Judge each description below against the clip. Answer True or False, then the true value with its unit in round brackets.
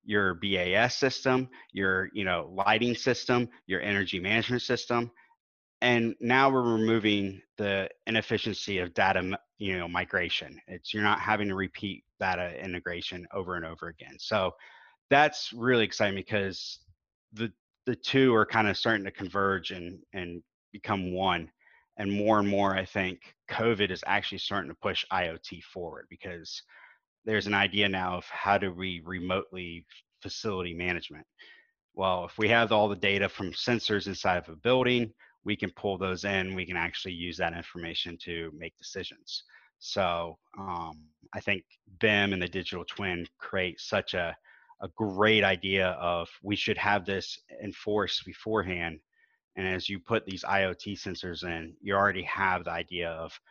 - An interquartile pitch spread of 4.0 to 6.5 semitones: False (3.2 semitones)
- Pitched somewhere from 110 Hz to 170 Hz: False (95 Hz)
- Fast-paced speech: False (160 wpm)